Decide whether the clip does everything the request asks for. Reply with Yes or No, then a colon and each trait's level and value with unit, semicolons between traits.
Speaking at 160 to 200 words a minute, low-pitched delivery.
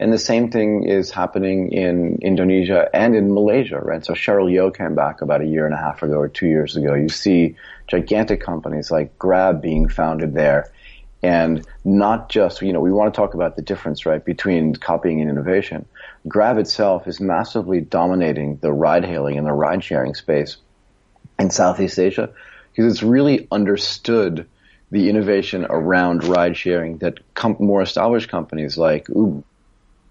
Yes: average, 165 wpm; very low, 90 Hz